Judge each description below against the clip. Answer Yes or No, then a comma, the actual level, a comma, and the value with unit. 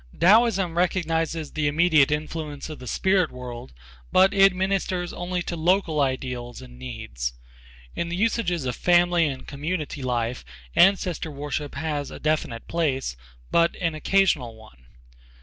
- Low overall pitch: No, medium, 155 Hz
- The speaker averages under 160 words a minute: Yes, average, 140 wpm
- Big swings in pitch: No, average, 5.0 semitones